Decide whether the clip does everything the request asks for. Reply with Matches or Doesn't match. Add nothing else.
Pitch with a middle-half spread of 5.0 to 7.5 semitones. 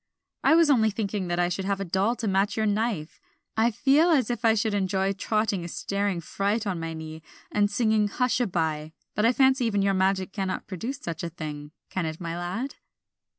Doesn't match